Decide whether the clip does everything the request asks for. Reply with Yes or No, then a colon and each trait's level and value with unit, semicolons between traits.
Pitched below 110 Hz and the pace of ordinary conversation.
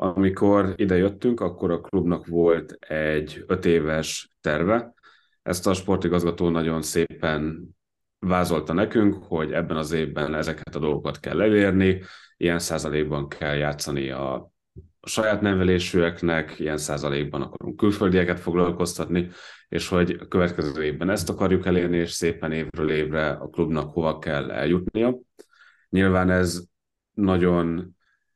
Yes: very low, 85 Hz; average, 125 wpm